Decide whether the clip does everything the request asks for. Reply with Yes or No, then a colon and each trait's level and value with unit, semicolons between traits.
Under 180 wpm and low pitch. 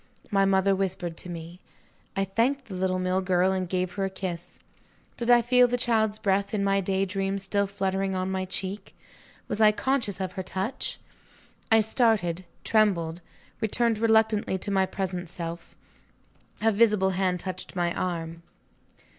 No: average, 165 wpm; high, 195 Hz